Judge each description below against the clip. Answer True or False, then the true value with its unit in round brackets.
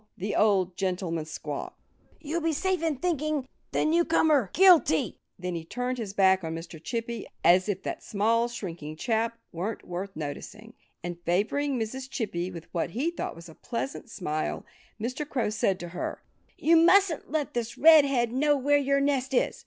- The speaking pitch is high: True (230 Hz)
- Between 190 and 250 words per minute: False (175 wpm)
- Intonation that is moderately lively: False (7.8 semitones)